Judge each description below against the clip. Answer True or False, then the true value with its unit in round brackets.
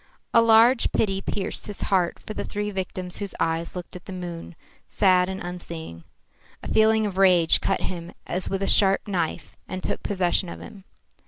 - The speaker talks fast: False (185 wpm)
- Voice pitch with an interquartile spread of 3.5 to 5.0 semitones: False (2.5 semitones)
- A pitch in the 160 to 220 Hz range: True (190 Hz)